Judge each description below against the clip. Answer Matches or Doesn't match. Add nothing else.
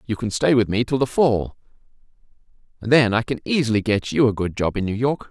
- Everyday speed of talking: Doesn't match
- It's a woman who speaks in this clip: Doesn't match